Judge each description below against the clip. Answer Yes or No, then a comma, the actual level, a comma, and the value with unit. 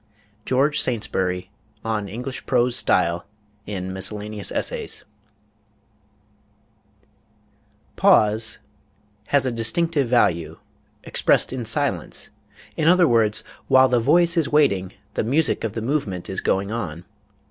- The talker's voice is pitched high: No, low, 115 Hz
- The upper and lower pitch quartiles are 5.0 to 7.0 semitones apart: Yes, wide, 5.6 semitones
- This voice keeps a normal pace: No, slow, 115 wpm